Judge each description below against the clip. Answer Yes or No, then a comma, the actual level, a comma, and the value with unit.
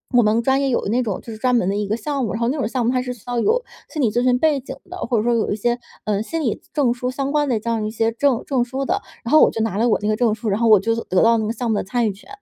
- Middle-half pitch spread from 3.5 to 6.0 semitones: No, average, 2.9 semitones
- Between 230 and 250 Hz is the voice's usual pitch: Yes, high, 235 Hz